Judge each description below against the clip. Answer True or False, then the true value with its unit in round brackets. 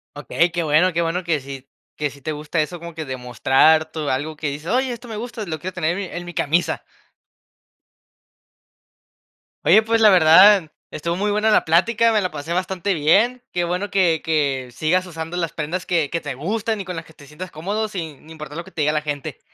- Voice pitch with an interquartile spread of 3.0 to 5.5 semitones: True (3.7 semitones)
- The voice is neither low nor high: True (170 Hz)